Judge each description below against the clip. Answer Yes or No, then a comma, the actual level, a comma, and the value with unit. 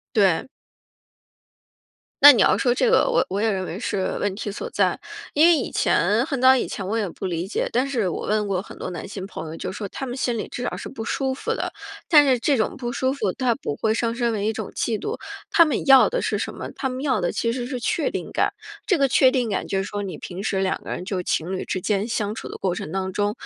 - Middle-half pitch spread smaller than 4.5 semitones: No, average, 5.2 semitones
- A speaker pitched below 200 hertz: No, high, 225 Hz